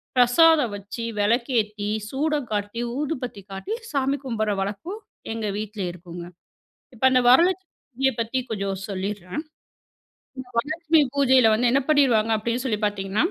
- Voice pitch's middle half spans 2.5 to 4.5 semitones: No, average, 5.0 semitones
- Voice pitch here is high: Yes, high, 235 Hz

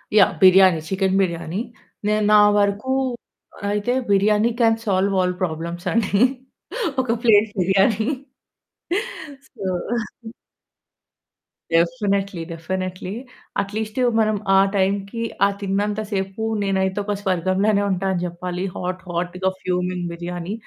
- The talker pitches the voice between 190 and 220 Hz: Yes, high, 195 Hz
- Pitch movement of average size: No, narrow, 2.3 semitones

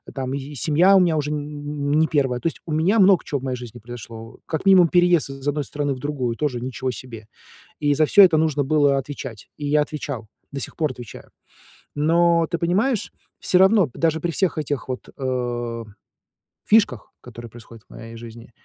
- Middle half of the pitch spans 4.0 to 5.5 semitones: Yes, average, 4.4 semitones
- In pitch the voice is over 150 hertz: No, medium, 145 Hz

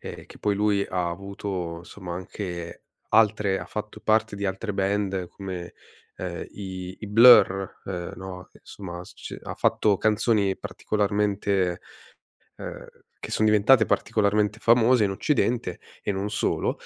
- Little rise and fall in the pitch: Yes, narrow, 2.2 semitones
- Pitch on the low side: Yes, low, 100 Hz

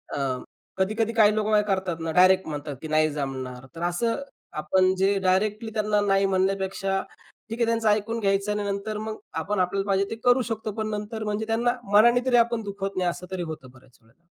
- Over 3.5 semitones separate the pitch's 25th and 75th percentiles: No, average, 2.9 semitones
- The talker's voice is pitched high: Yes, high, 200 Hz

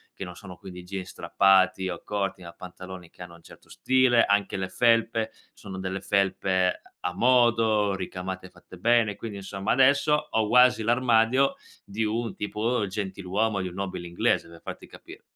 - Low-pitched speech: Yes, low, 100 Hz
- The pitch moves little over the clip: No, average, 3.5 semitones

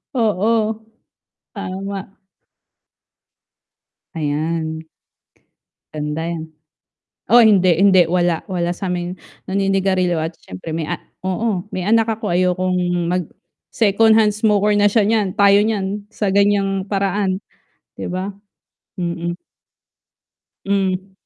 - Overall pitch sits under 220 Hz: Yes, high, 190 Hz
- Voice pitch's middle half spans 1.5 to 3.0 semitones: Yes, average, 2.7 semitones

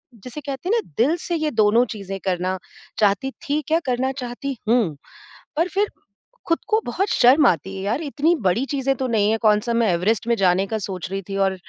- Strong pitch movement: Yes, wide, 6.3 semitones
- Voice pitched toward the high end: Yes, high, 235 Hz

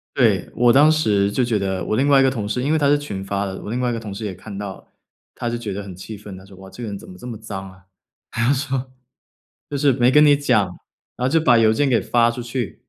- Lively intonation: No, average, 4.7 semitones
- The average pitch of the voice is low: Yes, low, 115 Hz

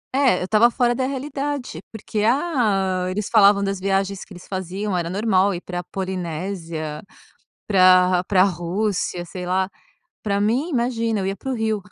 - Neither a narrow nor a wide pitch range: Yes, average, 3.6 semitones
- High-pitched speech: Yes, high, 195 Hz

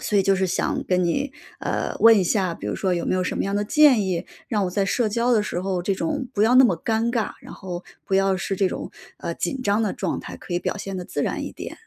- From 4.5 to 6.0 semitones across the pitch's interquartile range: No, average, 3.4 semitones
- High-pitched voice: Yes, high, 195 Hz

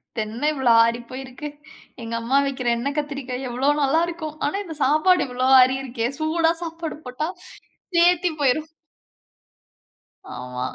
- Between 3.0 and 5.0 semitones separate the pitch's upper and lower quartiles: Yes, average, 4.0 semitones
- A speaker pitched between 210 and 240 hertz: No, very high, 275 Hz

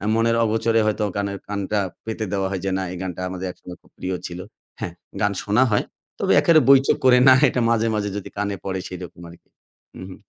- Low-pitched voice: Yes, low, 100 Hz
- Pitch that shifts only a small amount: No, average, 3.3 semitones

